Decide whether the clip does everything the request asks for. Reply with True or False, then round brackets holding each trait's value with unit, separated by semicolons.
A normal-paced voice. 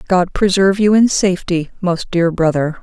True (170 wpm)